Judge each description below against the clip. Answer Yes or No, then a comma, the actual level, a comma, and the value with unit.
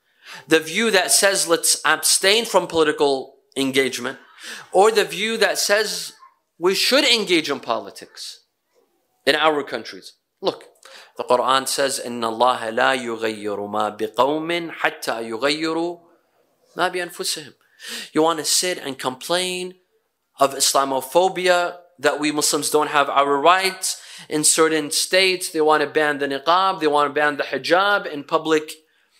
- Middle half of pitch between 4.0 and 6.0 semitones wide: Yes, average, 4.9 semitones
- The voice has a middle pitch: Yes, medium, 155 Hz